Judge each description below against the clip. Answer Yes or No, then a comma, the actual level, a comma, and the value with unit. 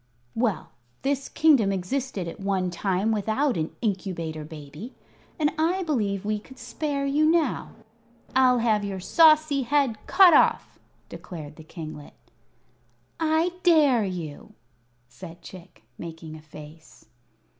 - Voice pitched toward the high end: Yes, high, 210 Hz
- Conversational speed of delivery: No, slow, 125 wpm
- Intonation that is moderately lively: No, wide, 8.7 semitones